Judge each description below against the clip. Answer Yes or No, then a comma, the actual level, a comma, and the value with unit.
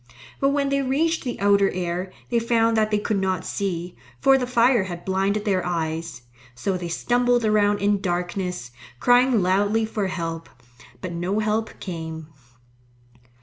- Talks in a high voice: Yes, high, 200 Hz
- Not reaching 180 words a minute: Yes, average, 155 wpm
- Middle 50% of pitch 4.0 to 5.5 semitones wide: Yes, average, 4.5 semitones